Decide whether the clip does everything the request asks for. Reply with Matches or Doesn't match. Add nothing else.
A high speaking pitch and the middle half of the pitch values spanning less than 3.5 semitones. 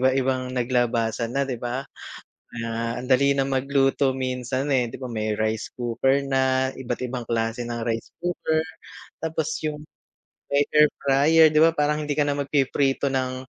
Doesn't match